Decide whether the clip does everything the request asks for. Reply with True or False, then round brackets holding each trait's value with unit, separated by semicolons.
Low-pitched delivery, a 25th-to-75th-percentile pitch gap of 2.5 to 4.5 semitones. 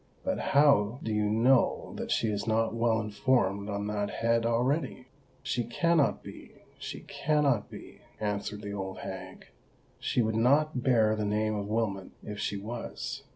True (110 Hz; 3.0 semitones)